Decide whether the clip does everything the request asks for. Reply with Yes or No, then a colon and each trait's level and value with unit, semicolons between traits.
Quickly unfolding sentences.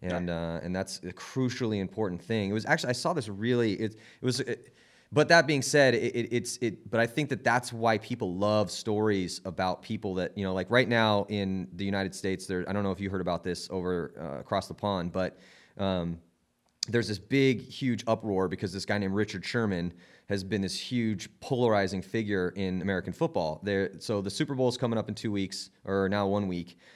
Yes: fast, 220 wpm